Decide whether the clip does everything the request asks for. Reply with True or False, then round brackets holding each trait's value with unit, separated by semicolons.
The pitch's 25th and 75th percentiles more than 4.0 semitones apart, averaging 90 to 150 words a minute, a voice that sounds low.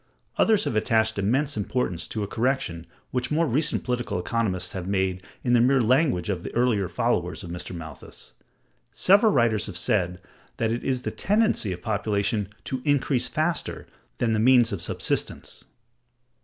False (5.4 semitones; 165 wpm; 115 Hz)